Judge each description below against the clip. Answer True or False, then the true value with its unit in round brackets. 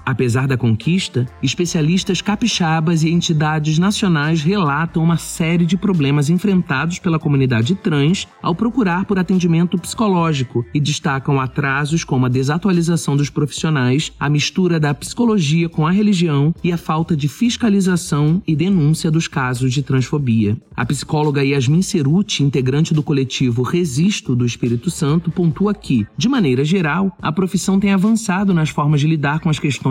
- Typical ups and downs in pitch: True (4.1 semitones)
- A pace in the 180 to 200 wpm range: False (150 wpm)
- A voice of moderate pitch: True (160 Hz)